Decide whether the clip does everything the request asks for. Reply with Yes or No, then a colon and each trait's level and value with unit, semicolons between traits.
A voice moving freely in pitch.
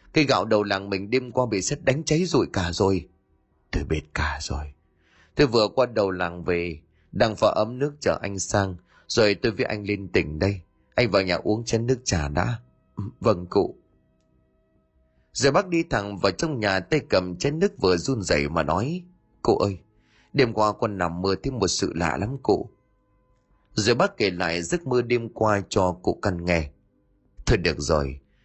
Yes: wide, 6.5 semitones